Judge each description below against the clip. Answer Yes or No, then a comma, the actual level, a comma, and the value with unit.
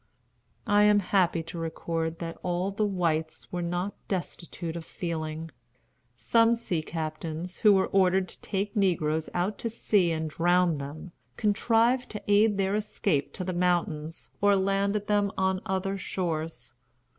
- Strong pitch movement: No, average, 3.5 semitones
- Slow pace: No, average, 150 wpm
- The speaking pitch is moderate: Yes, medium, 180 Hz